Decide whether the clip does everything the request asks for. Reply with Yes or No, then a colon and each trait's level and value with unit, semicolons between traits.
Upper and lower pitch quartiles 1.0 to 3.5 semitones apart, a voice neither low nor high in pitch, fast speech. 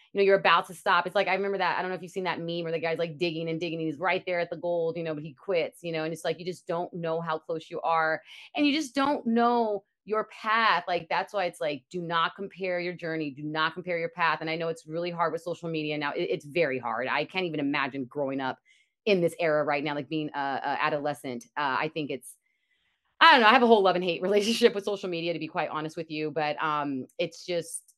Yes: average, 3.0 semitones; medium, 170 Hz; fast, 280 wpm